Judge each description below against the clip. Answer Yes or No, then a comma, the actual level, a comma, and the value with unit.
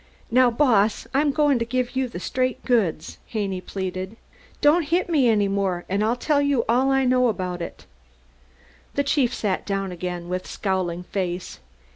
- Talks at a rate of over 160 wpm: Yes, average, 170 wpm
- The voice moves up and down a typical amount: No, wide, 5.8 semitones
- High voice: Yes, high, 225 Hz